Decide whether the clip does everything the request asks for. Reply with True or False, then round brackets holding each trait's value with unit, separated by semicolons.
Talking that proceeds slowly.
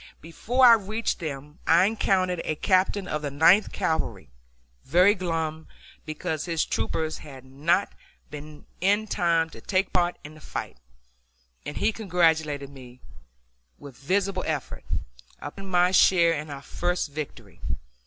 False (145 wpm)